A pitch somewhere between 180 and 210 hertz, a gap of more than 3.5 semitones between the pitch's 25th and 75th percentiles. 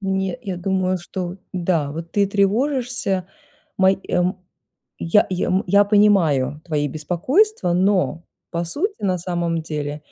No: medium, 185 Hz; average, 3.0 semitones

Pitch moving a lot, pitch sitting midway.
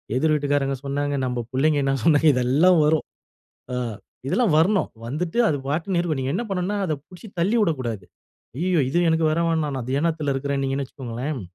No: average, 3.7 semitones; medium, 150 Hz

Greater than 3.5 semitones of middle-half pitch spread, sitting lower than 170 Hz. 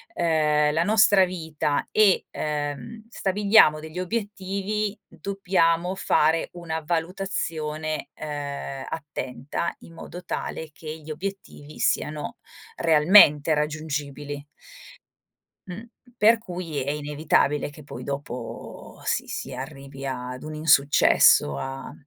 Yes: average, 3.9 semitones; medium, 155 Hz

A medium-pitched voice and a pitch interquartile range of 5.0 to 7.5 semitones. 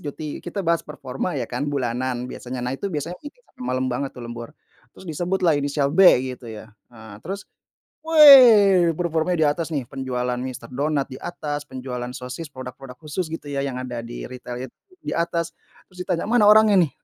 Yes: medium, 145 Hz; wide, 5.5 semitones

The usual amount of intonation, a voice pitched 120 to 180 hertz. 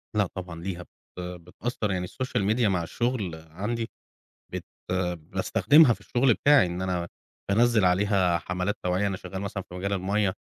No: average, 3.1 semitones; very low, 95 Hz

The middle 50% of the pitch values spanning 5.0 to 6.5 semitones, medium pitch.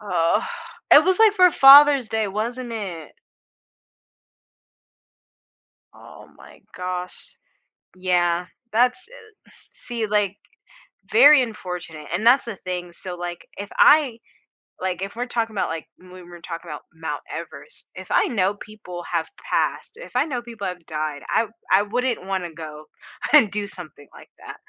No: wide, 5.6 semitones; high, 200 Hz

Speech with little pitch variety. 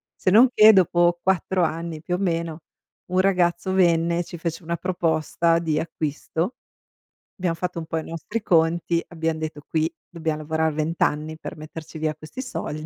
Yes: narrow, 2.0 semitones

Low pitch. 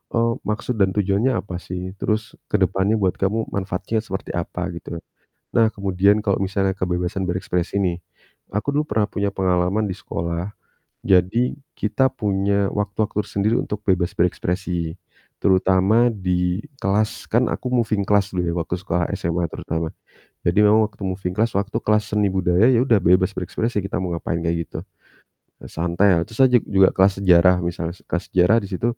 Yes: very low, 95 Hz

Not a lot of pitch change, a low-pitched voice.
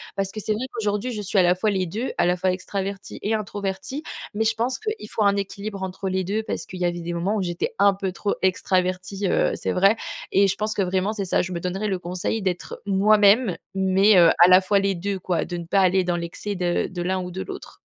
No: narrow, 2.2 semitones; high, 195 Hz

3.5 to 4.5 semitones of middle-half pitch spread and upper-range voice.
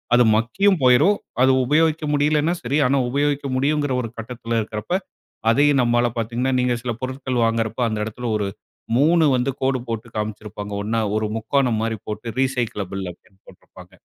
No: average, 3.9 semitones; low, 125 Hz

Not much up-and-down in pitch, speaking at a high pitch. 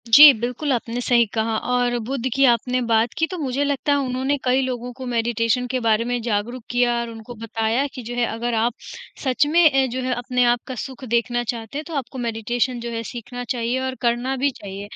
Yes: narrow, 2.0 semitones; high, 245 Hz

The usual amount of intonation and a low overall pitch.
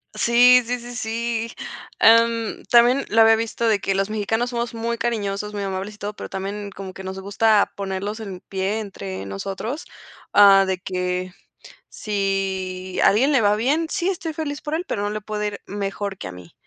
No: average, 3.2 semitones; high, 210 Hz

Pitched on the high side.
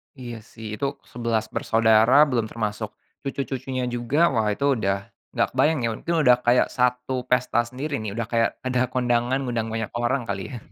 No: low, 120 Hz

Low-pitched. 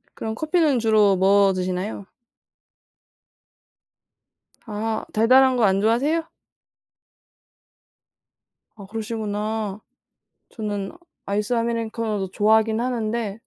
No: high, 220 Hz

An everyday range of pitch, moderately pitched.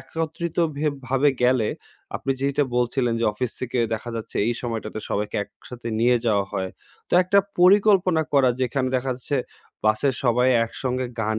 No: average, 3.6 semitones; low, 125 Hz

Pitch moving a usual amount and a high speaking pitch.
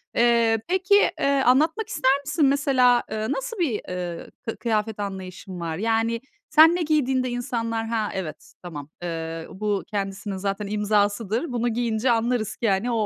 Yes: average, 4.3 semitones; high, 225 Hz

